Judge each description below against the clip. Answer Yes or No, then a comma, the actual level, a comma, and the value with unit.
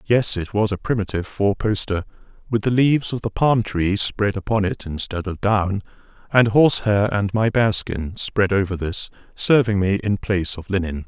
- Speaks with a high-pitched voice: No, low, 100 Hz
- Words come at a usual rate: Yes, average, 185 wpm